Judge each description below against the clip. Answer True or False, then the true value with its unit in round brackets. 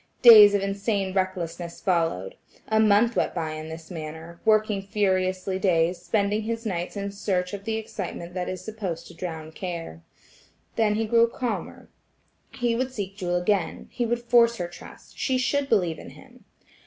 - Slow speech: False (165 wpm)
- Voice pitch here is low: False (195 Hz)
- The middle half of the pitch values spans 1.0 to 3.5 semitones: False (4.0 semitones)